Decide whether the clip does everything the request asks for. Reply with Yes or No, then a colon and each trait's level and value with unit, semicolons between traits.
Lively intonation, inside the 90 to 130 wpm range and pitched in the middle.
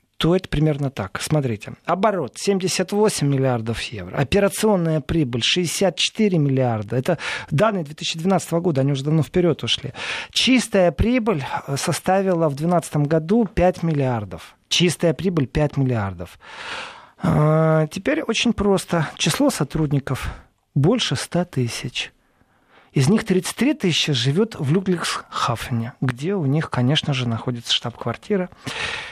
Yes: wide, 5.7 semitones; average, 115 wpm; medium, 160 Hz